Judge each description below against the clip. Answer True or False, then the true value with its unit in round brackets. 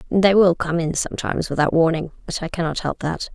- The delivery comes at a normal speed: False (215 wpm)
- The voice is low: False (170 Hz)